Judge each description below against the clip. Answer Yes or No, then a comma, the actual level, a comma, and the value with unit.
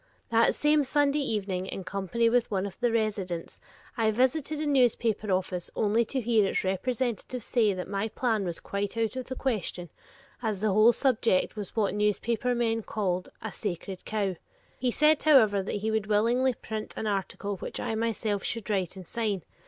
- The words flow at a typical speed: Yes, average, 185 wpm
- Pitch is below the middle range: No, high, 220 Hz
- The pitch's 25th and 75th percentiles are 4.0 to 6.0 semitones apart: No, average, 3.4 semitones